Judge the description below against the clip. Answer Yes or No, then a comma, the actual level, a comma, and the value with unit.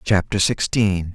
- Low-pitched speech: Yes, very low, 95 Hz